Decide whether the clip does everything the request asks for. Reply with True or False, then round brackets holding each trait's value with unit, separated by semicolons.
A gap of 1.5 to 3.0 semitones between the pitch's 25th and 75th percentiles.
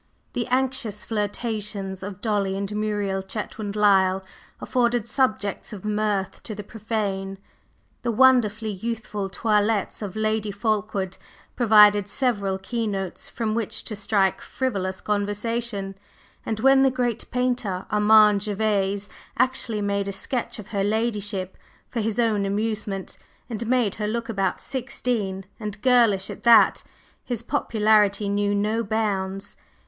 True (2.4 semitones)